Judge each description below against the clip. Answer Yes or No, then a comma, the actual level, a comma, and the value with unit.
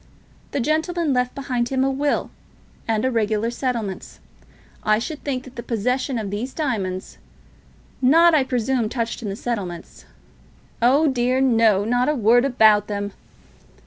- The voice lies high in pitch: Yes, high, 245 Hz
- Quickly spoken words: No, average, 155 wpm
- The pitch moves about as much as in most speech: Yes, average, 3.6 semitones